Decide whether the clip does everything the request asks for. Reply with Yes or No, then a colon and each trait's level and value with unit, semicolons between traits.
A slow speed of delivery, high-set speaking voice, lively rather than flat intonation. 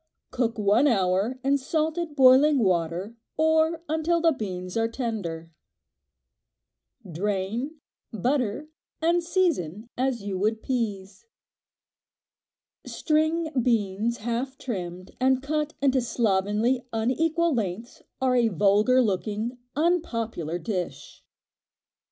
Yes: slow, 100 wpm; high, 235 Hz; wide, 6.2 semitones